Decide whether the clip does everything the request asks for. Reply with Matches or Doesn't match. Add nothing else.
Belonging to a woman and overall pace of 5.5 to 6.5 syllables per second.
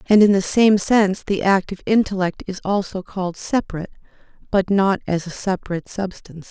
Matches